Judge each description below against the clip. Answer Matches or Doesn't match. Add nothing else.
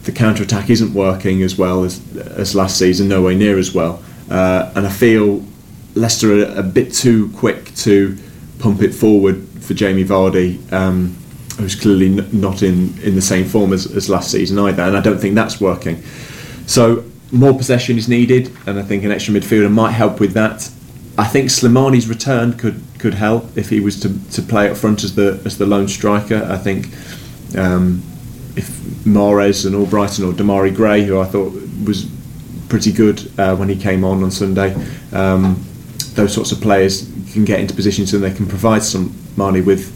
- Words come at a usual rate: Matches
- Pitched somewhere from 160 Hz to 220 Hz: Doesn't match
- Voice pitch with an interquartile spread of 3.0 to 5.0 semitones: Doesn't match